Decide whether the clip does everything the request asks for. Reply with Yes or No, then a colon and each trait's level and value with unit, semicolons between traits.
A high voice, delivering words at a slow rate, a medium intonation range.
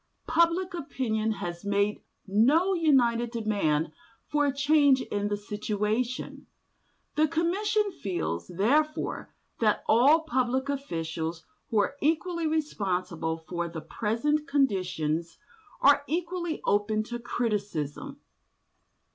No: high, 235 Hz; slow, 105 wpm; wide, 7.1 semitones